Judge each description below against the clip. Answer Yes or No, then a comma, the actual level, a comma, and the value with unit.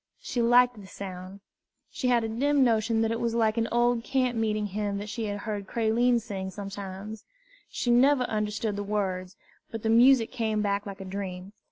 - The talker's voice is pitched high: Yes, high, 220 Hz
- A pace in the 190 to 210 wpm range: Yes, average, 195 wpm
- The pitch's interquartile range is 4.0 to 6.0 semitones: No, average, 2.9 semitones